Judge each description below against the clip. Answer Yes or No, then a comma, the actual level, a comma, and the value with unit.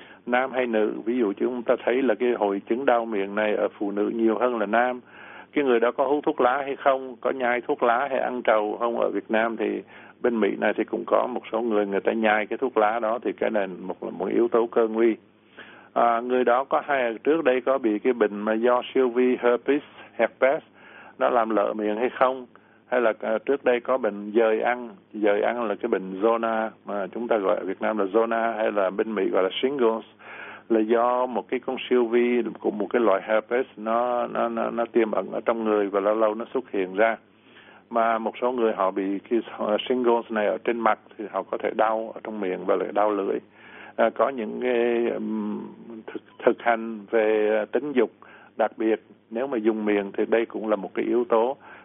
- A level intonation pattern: Yes, narrow, 2.3 semitones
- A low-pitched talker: Yes, low, 115 Hz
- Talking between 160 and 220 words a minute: No, average, 230 wpm